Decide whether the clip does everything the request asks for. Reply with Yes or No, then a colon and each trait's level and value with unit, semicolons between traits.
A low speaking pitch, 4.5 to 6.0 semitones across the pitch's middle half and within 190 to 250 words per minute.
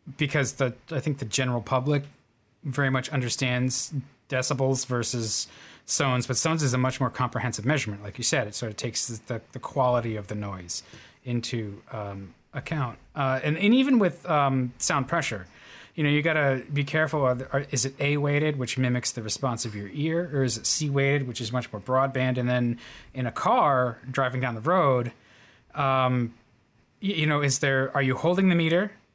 No: low, 130 Hz; average, 3.0 semitones; average, 200 wpm